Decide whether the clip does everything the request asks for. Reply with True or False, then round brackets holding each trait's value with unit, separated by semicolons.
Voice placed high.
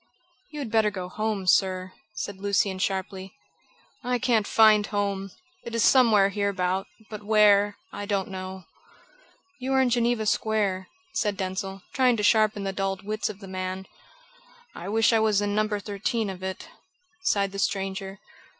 True (205 Hz)